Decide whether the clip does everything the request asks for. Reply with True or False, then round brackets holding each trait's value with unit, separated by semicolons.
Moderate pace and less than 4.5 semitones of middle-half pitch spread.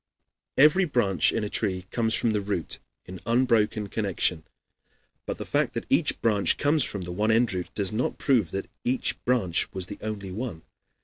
True (190 wpm; 4.1 semitones)